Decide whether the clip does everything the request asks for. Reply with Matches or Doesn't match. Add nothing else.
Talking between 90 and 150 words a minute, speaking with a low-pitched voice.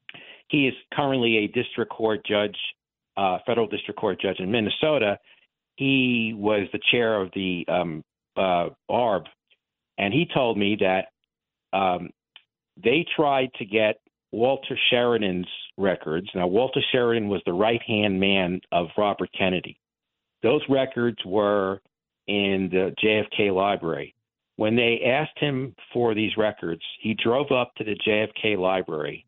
Matches